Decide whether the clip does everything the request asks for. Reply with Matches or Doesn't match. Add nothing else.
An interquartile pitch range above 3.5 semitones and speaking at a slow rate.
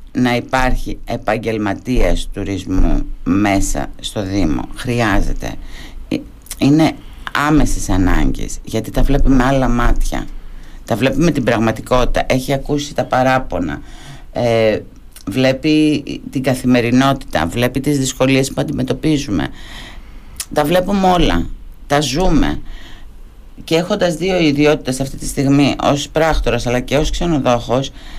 Matches